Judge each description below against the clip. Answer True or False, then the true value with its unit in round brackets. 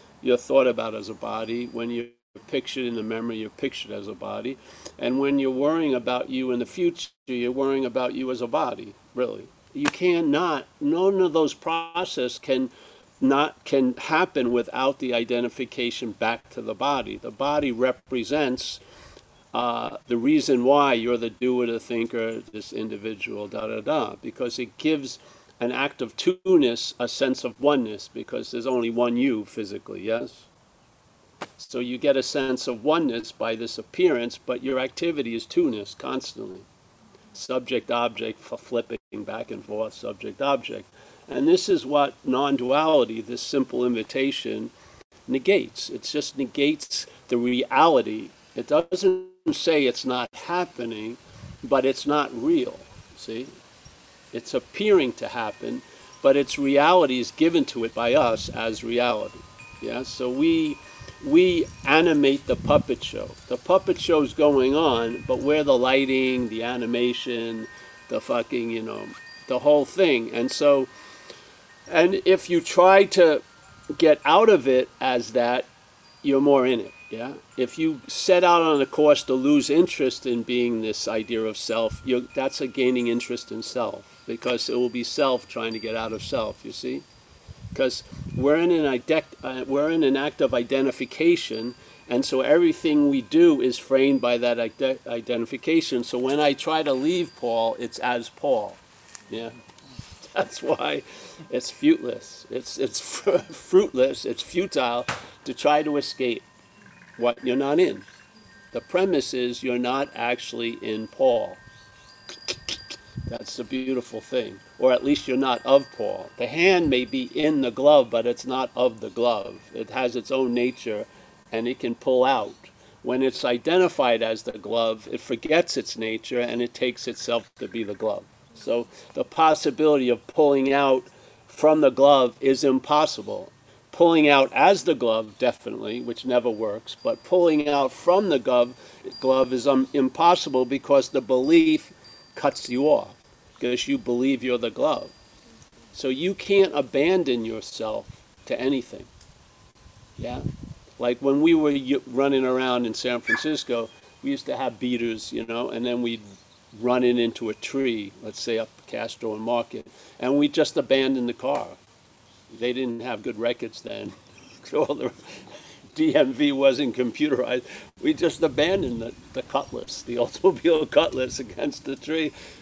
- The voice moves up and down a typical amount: True (3.9 semitones)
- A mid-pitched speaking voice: False (130 Hz)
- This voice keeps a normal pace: True (155 wpm)